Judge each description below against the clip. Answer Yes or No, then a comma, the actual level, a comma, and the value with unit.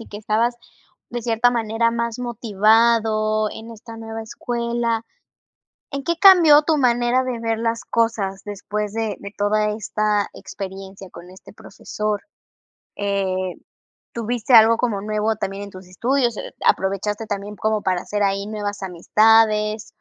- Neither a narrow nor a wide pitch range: No, narrow, 2.3 semitones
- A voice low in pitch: No, high, 215 Hz